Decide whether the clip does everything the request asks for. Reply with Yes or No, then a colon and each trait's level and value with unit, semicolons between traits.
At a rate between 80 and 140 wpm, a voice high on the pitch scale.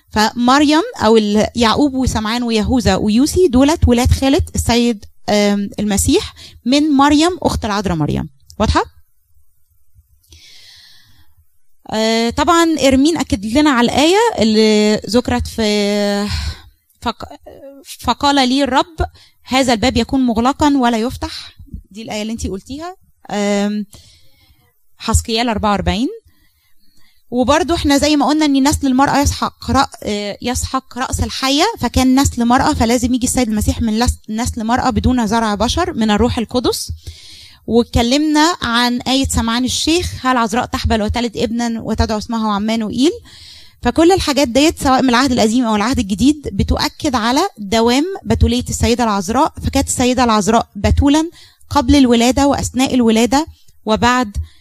Yes: average, 120 wpm; high, 240 Hz